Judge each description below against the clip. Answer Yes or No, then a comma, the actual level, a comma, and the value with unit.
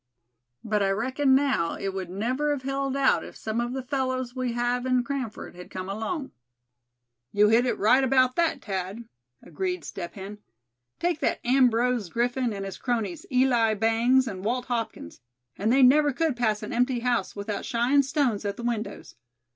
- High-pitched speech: Yes, high, 245 Hz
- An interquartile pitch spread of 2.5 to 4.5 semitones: Yes, average, 3.6 semitones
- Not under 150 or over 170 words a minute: No, average, 180 wpm